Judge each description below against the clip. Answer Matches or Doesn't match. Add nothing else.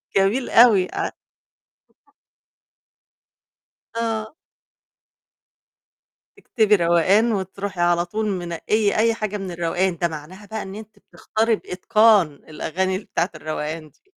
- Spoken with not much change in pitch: Doesn't match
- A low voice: Doesn't match